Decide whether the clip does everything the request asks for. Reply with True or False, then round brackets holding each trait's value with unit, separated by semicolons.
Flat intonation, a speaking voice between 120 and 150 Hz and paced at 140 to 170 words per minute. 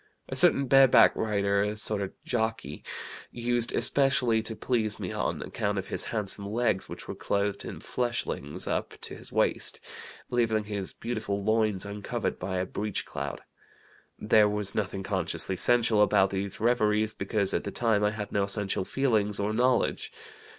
False (2.3 semitones; 105 Hz; 165 wpm)